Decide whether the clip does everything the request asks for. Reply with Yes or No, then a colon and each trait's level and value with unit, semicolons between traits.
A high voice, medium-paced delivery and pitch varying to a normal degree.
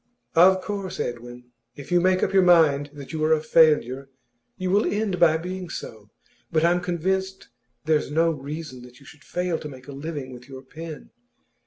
No: medium, 160 Hz; average, 190 wpm; average, 4.6 semitones